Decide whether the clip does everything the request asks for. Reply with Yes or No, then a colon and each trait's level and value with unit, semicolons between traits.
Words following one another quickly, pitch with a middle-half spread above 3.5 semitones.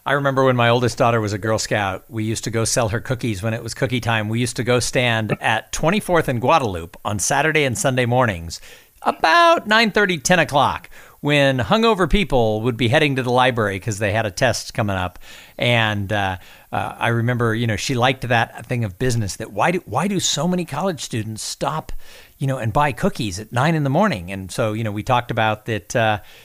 Yes: fast, 225 wpm; average, 4.1 semitones